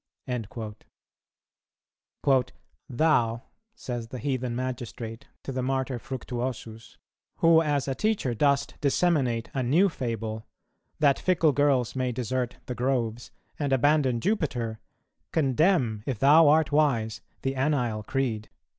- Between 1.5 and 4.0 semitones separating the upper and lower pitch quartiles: Yes, average, 3.5 semitones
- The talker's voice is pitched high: No, low, 130 Hz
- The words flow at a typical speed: No, slow, 120 wpm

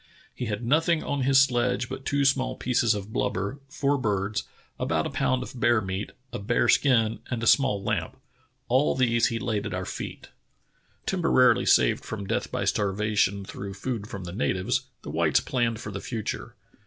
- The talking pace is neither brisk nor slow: Yes, average, 180 wpm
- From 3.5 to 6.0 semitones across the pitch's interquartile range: Yes, average, 4.2 semitones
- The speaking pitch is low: Yes, low, 115 Hz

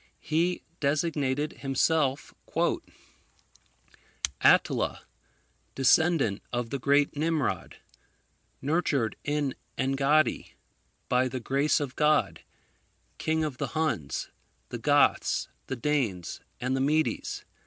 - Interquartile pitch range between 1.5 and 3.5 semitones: Yes, average, 2.8 semitones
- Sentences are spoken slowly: Yes, slow, 95 wpm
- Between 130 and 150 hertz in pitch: Yes, medium, 140 Hz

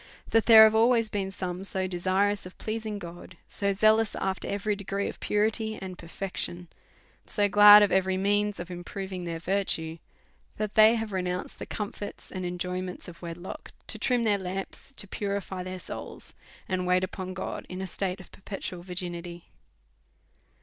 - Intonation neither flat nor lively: No, narrow, 2.3 semitones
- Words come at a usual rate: Yes, average, 170 wpm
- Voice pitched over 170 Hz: Yes, high, 190 Hz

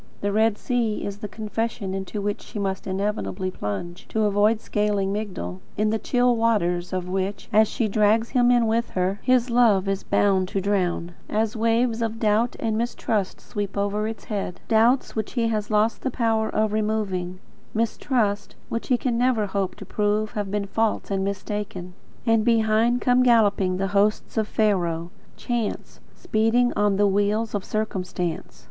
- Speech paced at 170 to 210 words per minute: Yes, average, 175 wpm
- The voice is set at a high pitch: Yes, high, 210 Hz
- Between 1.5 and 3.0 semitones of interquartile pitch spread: Yes, narrow, 2.4 semitones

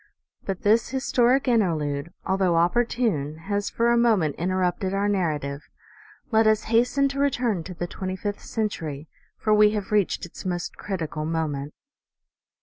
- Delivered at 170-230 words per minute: No, average, 145 wpm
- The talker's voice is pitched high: Yes, high, 195 Hz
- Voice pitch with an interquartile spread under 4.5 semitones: No, average, 5.3 semitones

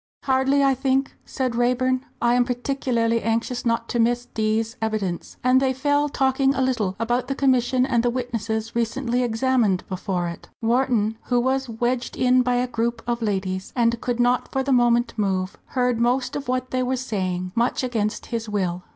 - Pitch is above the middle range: Yes, high, 240 Hz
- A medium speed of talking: Yes, average, 185 wpm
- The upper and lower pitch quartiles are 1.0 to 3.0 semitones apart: Yes, narrow, 2.4 semitones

